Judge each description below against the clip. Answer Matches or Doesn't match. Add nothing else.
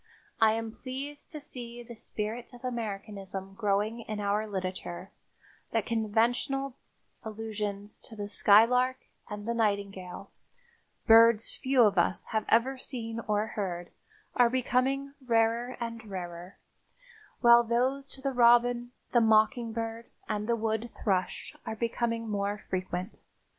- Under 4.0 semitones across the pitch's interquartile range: Matches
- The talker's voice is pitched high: Matches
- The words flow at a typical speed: Doesn't match